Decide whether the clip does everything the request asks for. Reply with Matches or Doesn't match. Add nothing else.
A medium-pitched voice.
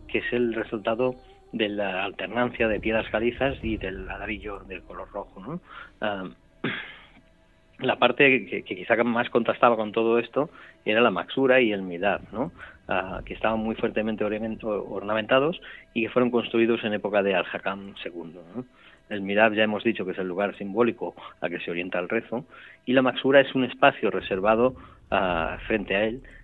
Doesn't match